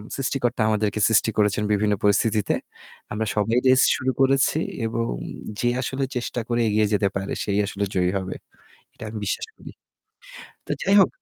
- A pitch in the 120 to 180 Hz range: No, low, 110 Hz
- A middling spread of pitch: Yes, average, 3.1 semitones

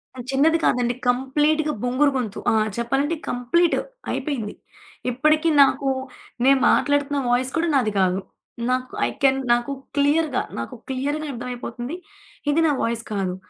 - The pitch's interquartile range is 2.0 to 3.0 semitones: No, average, 3.4 semitones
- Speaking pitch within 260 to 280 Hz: Yes, very high, 265 Hz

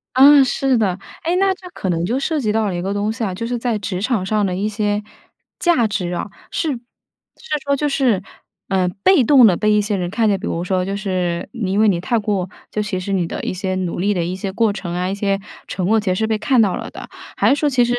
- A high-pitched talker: Yes, high, 210 Hz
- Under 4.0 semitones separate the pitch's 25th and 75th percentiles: No, average, 4.3 semitones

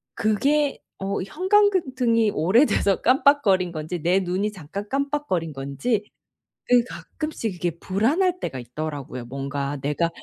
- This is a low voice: No, high, 200 Hz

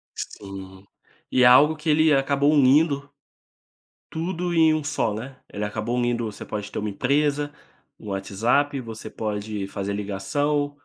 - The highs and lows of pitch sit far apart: Yes, wide, 5.8 semitones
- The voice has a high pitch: No, low, 130 Hz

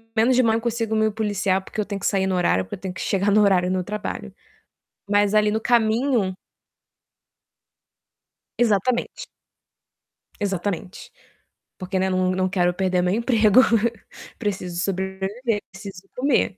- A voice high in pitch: Yes, high, 200 Hz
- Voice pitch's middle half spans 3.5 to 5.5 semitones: No, average, 2.8 semitones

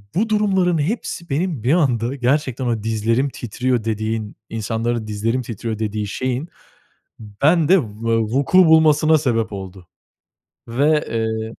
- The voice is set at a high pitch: No, low, 120 Hz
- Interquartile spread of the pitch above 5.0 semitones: Yes, wide, 5.4 semitones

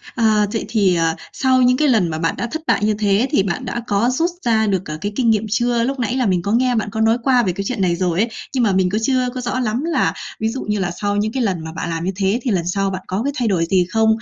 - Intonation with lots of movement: No, average, 4.3 semitones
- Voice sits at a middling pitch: No, high, 215 Hz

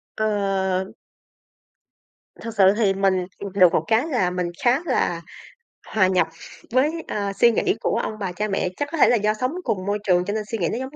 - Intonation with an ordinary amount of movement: Yes, average, 3.6 semitones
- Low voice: No, high, 205 Hz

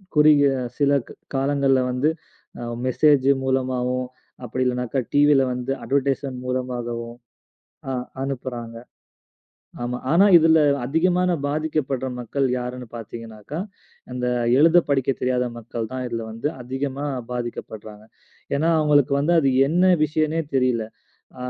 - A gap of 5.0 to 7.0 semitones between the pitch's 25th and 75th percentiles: No, average, 2.9 semitones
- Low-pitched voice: Yes, low, 130 Hz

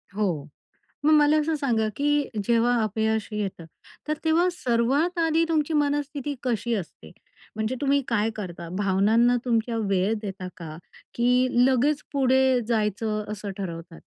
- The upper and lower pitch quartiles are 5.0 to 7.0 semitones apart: Yes, wide, 5.5 semitones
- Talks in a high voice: Yes, high, 235 Hz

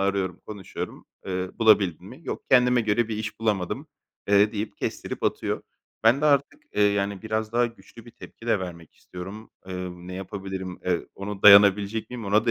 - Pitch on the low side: Yes, low, 105 Hz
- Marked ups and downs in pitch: No, average, 2.9 semitones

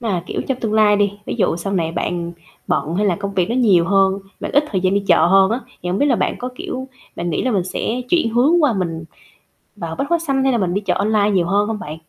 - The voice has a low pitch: No, high, 200 Hz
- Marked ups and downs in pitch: No, average, 5.0 semitones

